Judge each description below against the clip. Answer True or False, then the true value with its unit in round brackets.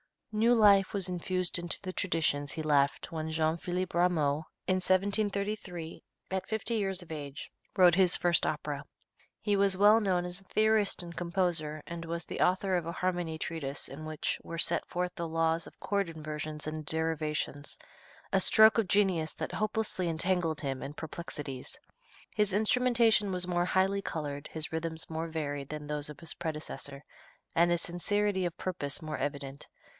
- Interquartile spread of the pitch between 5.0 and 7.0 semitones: False (3.4 semitones)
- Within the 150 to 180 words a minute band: True (170 wpm)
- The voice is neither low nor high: True (170 Hz)